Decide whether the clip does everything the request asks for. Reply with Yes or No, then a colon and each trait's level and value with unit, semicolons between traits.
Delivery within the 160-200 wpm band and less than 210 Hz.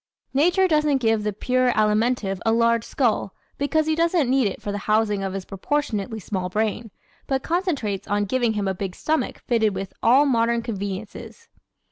No: average, 175 wpm; high, 225 Hz